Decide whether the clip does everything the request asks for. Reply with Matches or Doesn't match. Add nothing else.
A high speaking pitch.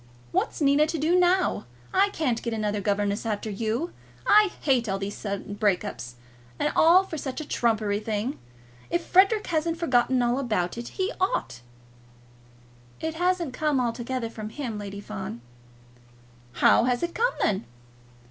Matches